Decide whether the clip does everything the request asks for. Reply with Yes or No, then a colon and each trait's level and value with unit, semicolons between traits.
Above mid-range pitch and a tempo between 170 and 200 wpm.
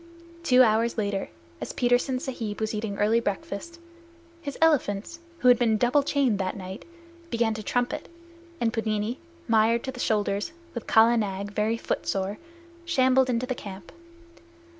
No: high, 230 Hz; average, 150 wpm